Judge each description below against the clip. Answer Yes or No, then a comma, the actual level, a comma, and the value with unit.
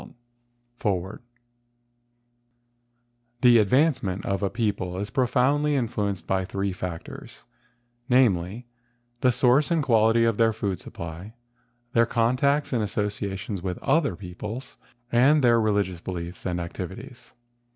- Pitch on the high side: No, low, 110 Hz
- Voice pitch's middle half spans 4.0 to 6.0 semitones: Yes, average, 4.6 semitones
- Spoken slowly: Yes, slow, 120 wpm